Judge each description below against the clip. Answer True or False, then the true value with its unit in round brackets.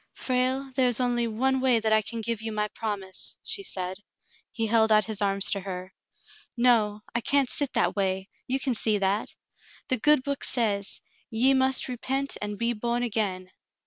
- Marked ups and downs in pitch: False (3.7 semitones)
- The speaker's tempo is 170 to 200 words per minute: True (185 wpm)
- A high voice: True (225 Hz)